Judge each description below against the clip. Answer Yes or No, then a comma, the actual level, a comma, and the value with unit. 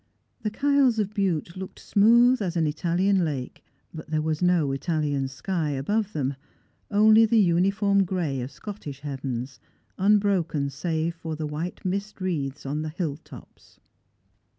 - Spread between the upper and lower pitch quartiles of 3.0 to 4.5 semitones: No, average, 5.2 semitones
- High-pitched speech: No, medium, 170 Hz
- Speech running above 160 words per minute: No, average, 150 wpm